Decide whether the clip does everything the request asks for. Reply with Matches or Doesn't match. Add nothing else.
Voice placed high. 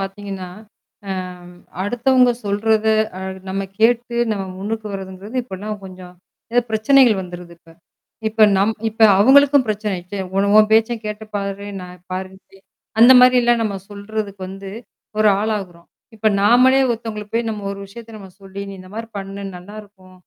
Matches